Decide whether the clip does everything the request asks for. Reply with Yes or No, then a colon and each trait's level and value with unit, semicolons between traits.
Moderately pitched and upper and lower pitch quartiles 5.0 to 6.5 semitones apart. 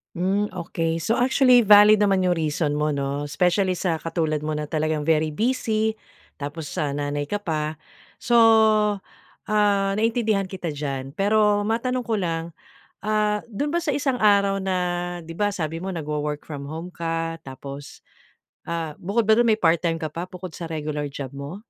Yes: medium, 175 Hz; wide, 5.4 semitones